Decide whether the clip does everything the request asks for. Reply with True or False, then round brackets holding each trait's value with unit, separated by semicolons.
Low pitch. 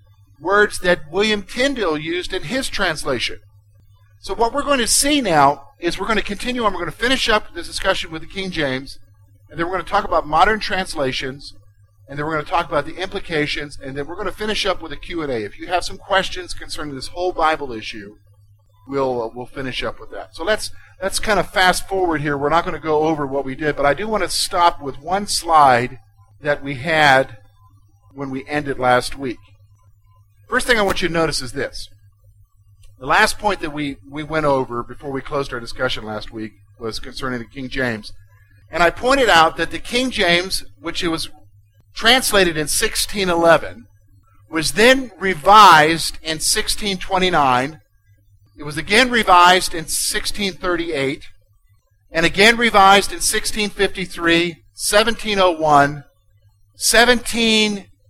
False (155 Hz)